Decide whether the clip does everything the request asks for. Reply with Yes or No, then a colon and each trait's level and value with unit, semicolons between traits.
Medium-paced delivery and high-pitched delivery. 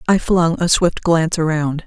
No: average, 195 wpm; medium, 165 Hz